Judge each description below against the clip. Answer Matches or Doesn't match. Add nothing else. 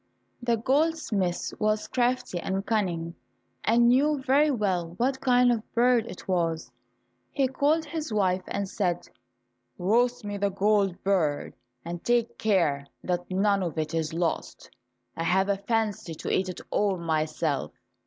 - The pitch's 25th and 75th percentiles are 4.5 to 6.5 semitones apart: Matches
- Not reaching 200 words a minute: Matches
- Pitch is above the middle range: Matches